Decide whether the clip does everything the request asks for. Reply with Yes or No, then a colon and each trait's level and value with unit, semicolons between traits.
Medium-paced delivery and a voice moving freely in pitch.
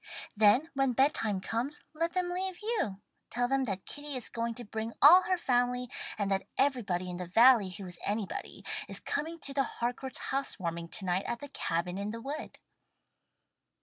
Yes: average, 180 wpm; wide, 6.0 semitones